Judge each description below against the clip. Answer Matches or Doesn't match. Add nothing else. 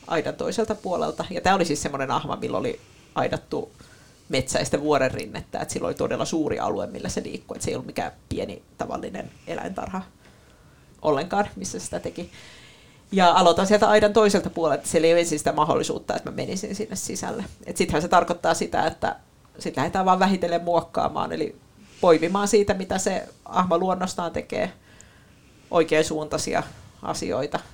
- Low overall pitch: Doesn't match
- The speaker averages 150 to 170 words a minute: Matches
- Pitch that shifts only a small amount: Doesn't match